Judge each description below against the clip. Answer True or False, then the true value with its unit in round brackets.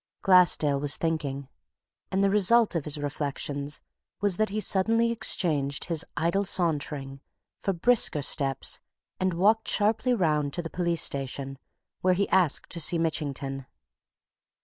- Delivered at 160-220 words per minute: False (140 wpm)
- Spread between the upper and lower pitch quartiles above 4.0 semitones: True (5.4 semitones)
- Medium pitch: True (165 Hz)